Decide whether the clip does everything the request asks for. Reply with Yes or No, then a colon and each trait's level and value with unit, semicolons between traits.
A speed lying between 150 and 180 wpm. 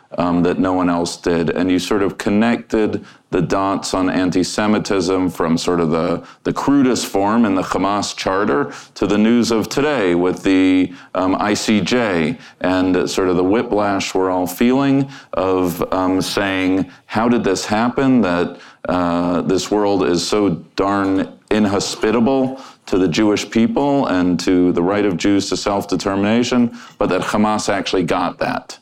Yes: average, 160 wpm